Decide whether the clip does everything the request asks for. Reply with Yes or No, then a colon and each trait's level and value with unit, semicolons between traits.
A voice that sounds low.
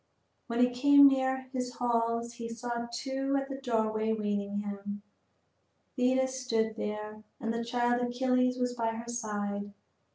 No: high, 235 Hz